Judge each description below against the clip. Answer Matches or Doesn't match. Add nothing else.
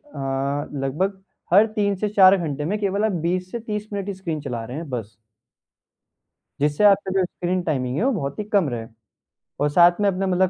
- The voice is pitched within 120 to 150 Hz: Doesn't match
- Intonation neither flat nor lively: Doesn't match